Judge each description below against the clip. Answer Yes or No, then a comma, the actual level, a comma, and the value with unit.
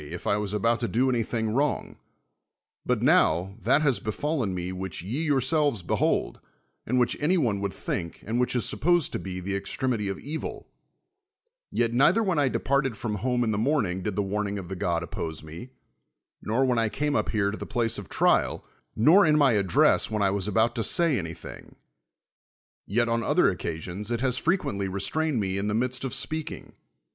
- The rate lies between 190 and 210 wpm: Yes, average, 195 wpm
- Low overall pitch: Yes, low, 115 Hz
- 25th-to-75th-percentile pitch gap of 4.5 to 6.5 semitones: Yes, average, 5.3 semitones